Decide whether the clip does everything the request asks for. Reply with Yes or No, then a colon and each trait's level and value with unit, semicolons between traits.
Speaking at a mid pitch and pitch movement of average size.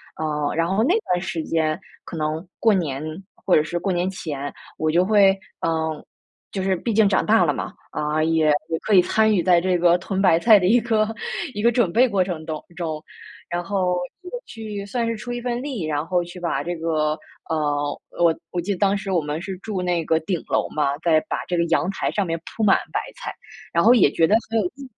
Yes: medium, 180 Hz; average, 4.2 semitones